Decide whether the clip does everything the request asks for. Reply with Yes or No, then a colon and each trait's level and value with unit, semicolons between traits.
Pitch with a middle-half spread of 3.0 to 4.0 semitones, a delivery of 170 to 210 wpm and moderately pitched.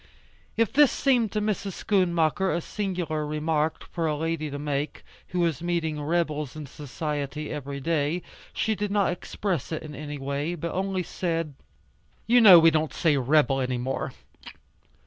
No: average, 3.6 semitones; average, 160 wpm; medium, 160 Hz